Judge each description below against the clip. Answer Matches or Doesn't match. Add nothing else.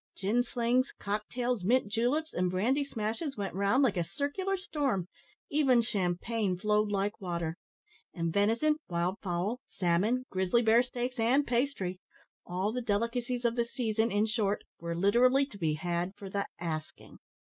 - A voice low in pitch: Doesn't match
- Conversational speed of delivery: Matches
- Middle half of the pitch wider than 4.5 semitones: Matches